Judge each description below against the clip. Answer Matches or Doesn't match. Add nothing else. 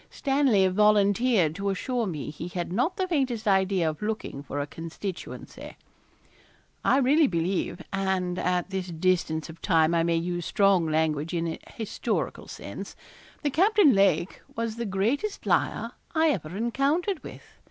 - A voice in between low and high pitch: Doesn't match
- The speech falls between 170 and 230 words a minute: Doesn't match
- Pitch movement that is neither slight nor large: Doesn't match